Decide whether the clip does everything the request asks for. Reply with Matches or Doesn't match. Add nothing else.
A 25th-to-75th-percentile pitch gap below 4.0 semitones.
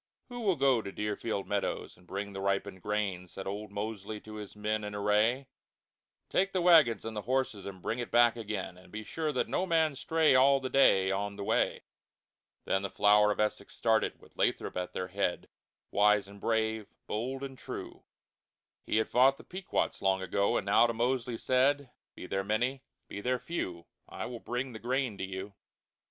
Doesn't match